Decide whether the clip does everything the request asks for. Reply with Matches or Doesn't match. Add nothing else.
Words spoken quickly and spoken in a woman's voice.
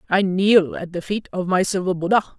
Matches